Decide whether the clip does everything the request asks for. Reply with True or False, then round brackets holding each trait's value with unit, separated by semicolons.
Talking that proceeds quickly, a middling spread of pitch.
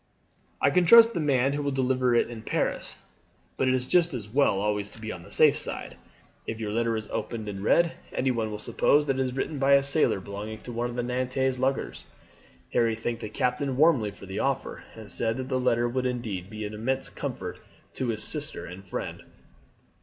True (215 wpm; 3.7 semitones)